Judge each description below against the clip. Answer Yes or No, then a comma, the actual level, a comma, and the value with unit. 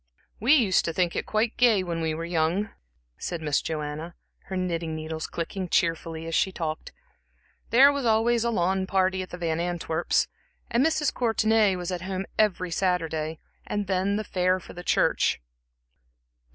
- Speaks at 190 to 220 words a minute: No, average, 170 wpm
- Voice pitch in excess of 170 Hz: Yes, medium, 185 Hz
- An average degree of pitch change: Yes, average, 4.1 semitones